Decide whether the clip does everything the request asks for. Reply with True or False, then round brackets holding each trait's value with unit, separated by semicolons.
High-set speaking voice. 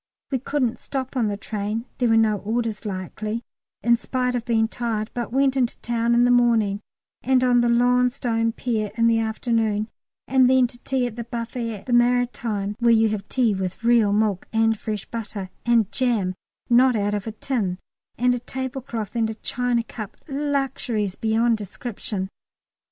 True (230 Hz)